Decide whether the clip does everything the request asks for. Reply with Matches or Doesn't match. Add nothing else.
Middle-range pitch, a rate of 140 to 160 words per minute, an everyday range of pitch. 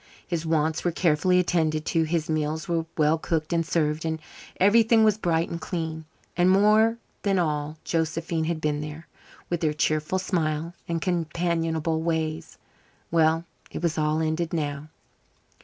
Doesn't match